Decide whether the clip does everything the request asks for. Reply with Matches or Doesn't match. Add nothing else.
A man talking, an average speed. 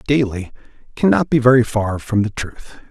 Matches